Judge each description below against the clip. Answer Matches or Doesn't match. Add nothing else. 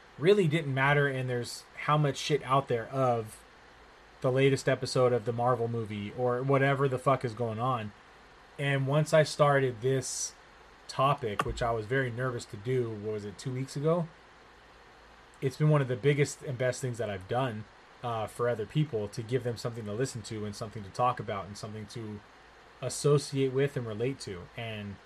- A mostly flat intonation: Doesn't match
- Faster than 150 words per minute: Matches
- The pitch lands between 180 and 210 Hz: Doesn't match